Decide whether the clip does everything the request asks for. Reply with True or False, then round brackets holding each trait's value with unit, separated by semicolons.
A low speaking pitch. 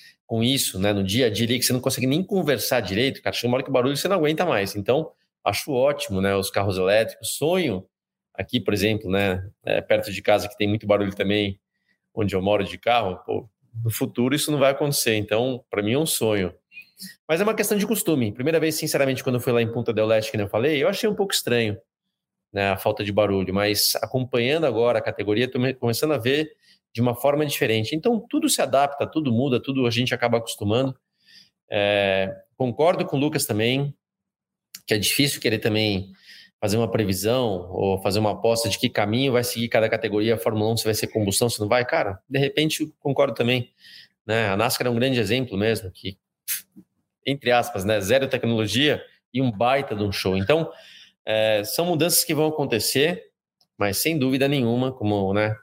True (120 Hz)